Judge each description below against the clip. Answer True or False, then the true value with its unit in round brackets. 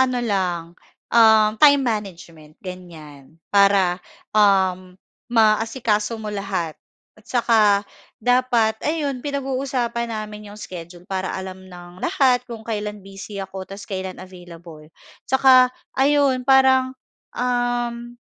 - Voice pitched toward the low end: False (210 Hz)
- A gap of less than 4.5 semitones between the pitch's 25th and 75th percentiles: False (4.8 semitones)